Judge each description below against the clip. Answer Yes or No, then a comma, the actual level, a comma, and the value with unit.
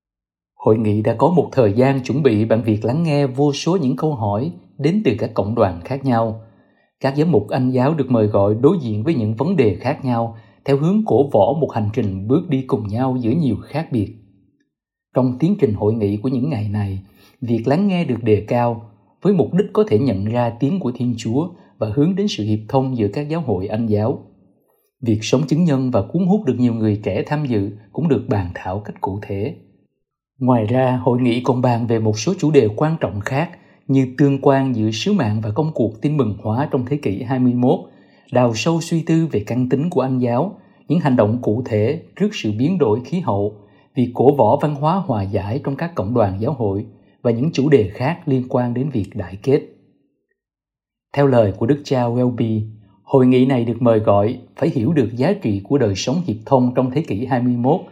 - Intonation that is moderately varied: Yes, average, 4.7 semitones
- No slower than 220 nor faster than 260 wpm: Yes, average, 225 wpm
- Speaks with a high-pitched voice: No, low, 125 Hz